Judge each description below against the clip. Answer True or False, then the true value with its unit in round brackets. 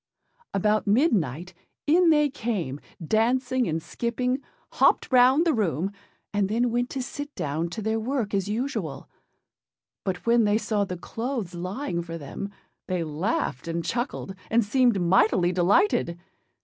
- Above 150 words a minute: False (145 wpm)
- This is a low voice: False (215 Hz)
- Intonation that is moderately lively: False (5.9 semitones)